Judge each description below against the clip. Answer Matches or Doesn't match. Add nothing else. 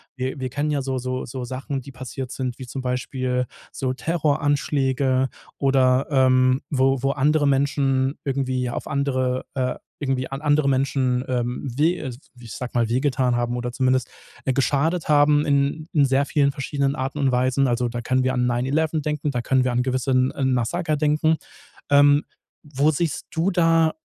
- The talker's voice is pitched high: Doesn't match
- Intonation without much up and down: Matches